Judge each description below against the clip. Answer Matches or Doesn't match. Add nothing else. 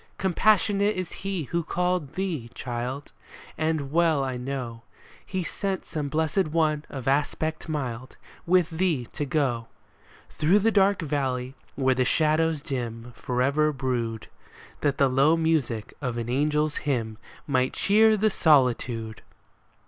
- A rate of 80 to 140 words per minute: Matches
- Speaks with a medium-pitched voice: Matches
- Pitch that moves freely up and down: Doesn't match